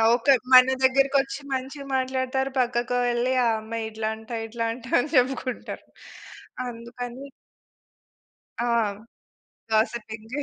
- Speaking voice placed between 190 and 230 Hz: No, very high, 250 Hz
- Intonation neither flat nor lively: No, narrow, 2.3 semitones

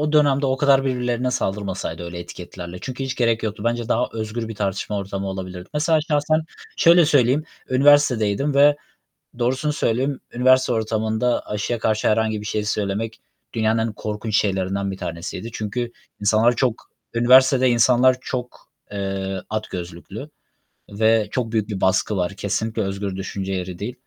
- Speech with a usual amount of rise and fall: Yes, average, 4.4 semitones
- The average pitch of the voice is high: No, low, 110 Hz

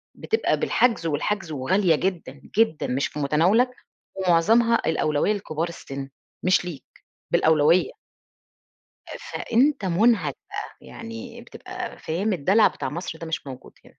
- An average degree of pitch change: No, wide, 6.4 semitones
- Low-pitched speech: No, medium, 185 Hz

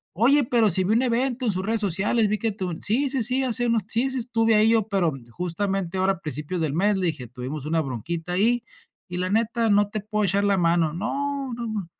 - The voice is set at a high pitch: Yes, high, 205 Hz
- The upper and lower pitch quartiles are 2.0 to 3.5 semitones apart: No, average, 4.5 semitones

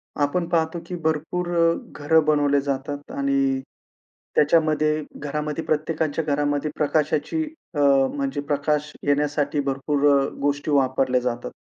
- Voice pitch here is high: No, medium, 145 Hz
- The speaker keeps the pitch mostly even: Yes, narrow, 1.7 semitones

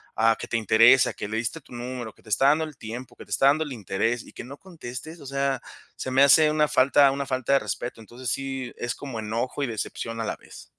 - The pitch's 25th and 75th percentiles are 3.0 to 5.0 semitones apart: Yes, average, 3.3 semitones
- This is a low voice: Yes, low, 130 Hz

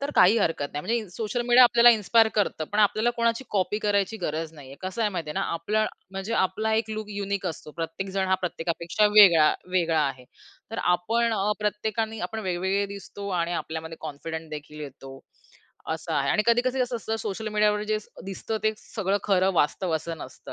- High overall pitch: Yes, high, 200 Hz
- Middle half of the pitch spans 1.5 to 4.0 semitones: No, average, 4.8 semitones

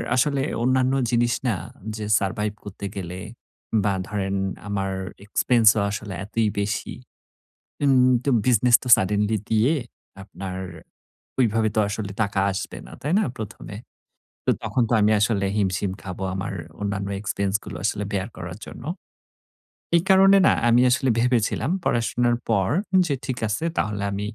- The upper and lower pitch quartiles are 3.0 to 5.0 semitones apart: Yes, average, 3.5 semitones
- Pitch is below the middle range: Yes, low, 105 Hz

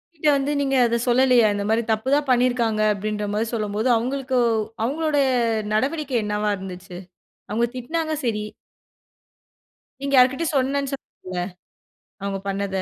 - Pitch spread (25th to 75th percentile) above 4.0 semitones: Yes, average, 4.6 semitones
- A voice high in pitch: Yes, high, 240 Hz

